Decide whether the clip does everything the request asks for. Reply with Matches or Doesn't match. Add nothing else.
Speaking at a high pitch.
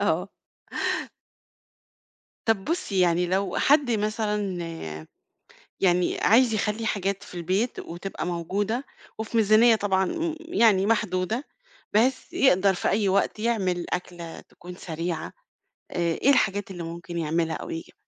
Matches